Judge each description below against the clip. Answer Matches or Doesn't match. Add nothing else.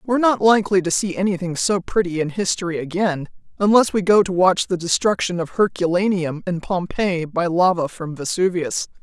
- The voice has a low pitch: Doesn't match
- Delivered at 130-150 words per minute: Doesn't match